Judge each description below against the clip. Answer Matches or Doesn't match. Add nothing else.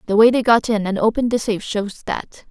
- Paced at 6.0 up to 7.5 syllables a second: Matches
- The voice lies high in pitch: Matches